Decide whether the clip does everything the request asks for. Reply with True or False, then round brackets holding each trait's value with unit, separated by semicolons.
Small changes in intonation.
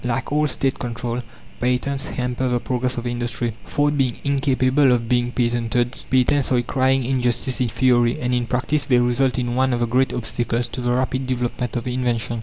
True (1.4 semitones)